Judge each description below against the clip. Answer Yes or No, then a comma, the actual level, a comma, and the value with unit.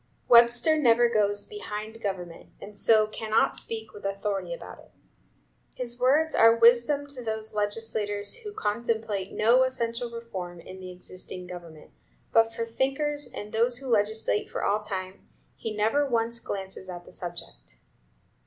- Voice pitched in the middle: No, high, 220 Hz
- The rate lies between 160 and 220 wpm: No, average, 150 wpm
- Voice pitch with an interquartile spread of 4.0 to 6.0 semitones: No, average, 2.9 semitones